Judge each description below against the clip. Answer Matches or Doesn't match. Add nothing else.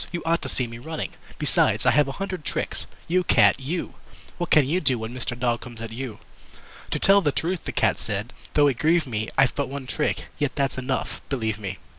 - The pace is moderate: Doesn't match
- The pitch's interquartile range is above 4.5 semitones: Matches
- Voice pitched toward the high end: Doesn't match